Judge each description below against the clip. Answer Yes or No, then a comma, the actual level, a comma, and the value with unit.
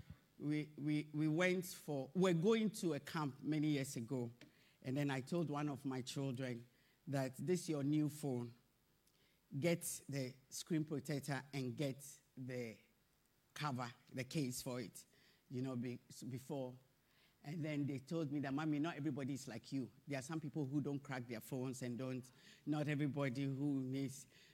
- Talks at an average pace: Yes, average, 175 wpm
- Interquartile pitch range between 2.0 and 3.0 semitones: Yes, average, 2.7 semitones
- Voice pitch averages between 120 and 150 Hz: Yes, medium, 140 Hz